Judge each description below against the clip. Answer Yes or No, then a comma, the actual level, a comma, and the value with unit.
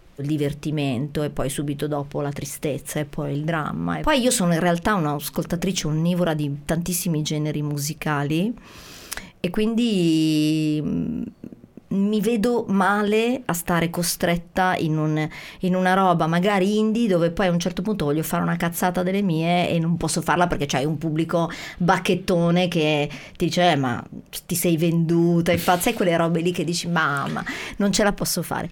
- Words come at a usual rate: No, fast, 175 wpm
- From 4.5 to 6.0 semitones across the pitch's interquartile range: No, average, 3.2 semitones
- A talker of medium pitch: Yes, medium, 170 Hz